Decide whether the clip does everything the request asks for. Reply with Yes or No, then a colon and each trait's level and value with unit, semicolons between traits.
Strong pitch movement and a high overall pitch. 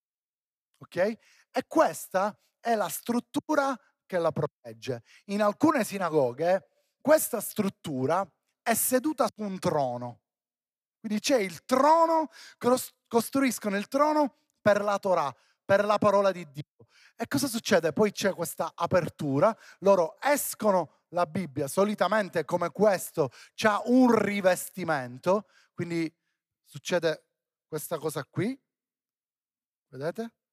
Yes: wide, 6.0 semitones; high, 200 Hz